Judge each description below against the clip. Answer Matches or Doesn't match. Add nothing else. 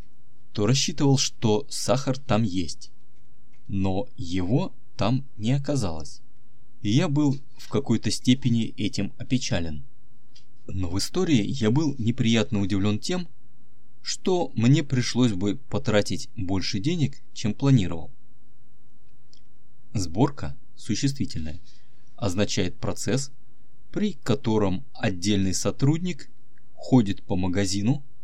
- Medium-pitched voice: Doesn't match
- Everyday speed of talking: Doesn't match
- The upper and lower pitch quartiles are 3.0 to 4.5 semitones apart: Matches